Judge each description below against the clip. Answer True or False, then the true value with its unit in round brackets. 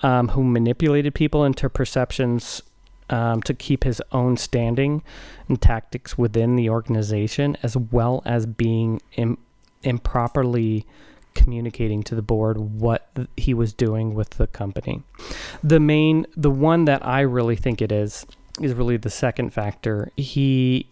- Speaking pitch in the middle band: False (120 Hz)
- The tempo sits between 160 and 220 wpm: False (145 wpm)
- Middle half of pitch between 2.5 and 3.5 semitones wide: True (3.0 semitones)